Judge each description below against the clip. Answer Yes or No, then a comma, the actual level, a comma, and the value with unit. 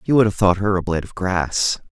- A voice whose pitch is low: Yes, very low, 95 Hz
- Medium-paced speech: No, fast, 280 wpm